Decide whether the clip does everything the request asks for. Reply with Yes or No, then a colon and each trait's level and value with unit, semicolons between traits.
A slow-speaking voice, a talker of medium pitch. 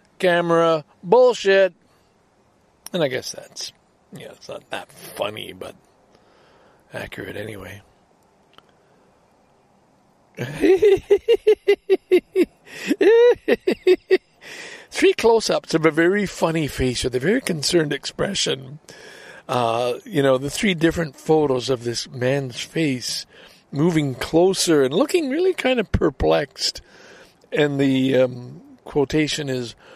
Yes: slow, 100 wpm; medium, 170 Hz